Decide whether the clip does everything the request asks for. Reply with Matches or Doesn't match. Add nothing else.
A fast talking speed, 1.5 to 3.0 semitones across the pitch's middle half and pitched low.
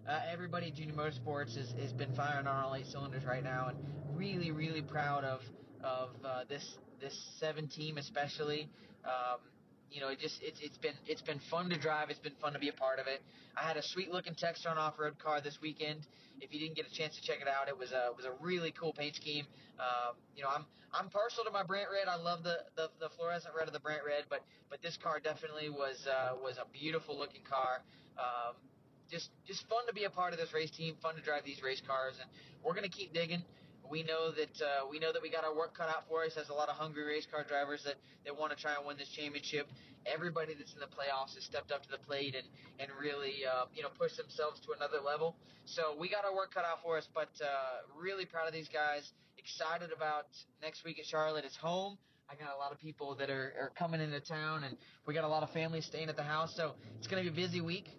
Doesn't match